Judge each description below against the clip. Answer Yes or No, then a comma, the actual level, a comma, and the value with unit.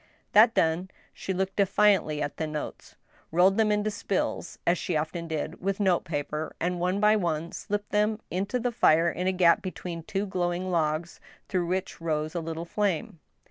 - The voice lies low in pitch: No, medium, 180 Hz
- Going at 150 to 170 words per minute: No, average, 180 wpm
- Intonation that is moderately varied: Yes, average, 3.5 semitones